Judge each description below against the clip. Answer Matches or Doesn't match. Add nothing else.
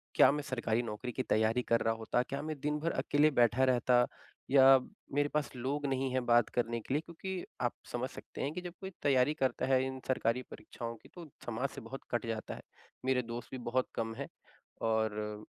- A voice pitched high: Doesn't match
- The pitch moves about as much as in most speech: Matches